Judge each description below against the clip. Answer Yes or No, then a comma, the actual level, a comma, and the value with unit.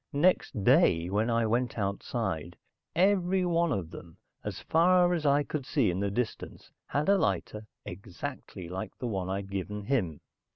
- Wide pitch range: Yes, wide, 7.8 semitones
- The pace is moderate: Yes, average, 160 wpm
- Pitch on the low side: Yes, low, 110 Hz